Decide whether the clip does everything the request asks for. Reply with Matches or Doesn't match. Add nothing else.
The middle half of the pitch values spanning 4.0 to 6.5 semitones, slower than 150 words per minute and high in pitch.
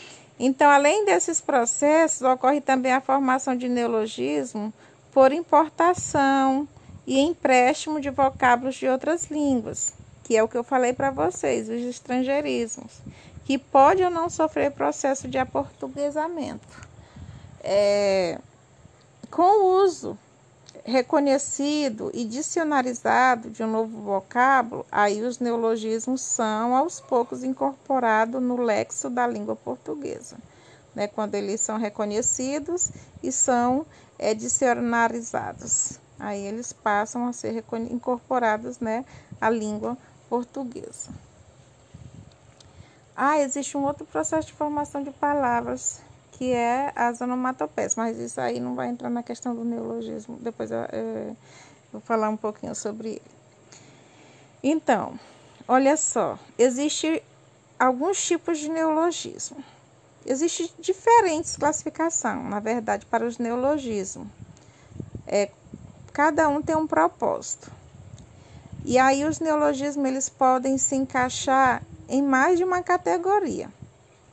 Matches